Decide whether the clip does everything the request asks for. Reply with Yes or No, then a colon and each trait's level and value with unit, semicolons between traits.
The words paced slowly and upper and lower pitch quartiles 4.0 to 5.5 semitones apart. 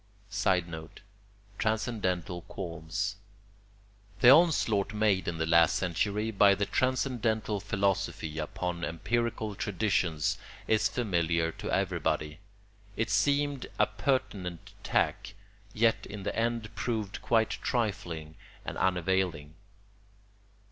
Yes: slow, 100 wpm; average, 4.3 semitones